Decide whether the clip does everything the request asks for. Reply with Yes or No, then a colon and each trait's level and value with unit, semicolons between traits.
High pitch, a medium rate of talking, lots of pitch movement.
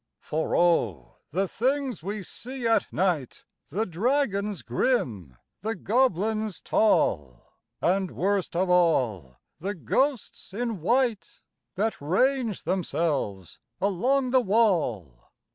No: high, 195 Hz; slow, 110 wpm; wide, 6.5 semitones